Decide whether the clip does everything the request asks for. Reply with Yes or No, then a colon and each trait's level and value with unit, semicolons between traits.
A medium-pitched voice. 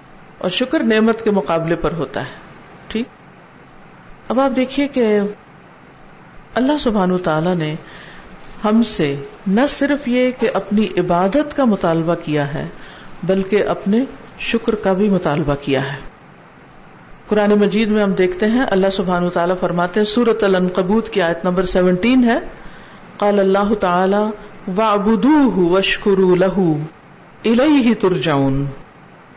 No: high, 195 Hz